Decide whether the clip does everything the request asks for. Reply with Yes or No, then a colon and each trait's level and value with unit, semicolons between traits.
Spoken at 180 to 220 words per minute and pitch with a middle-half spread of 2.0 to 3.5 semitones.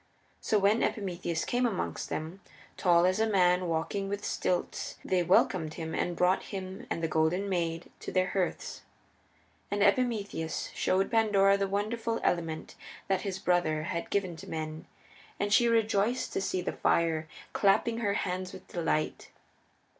No: average, 155 wpm; average, 3.1 semitones